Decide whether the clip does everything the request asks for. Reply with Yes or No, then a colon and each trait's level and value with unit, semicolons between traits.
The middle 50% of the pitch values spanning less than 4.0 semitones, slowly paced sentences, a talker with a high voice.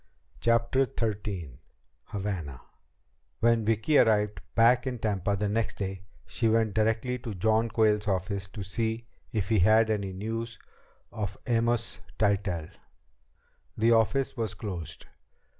No: narrow, 2.5 semitones; slow, 125 wpm; low, 110 Hz